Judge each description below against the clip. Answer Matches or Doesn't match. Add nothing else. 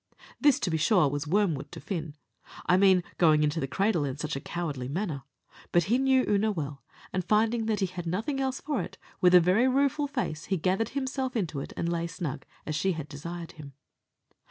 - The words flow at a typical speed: Doesn't match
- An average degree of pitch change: Doesn't match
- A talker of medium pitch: Matches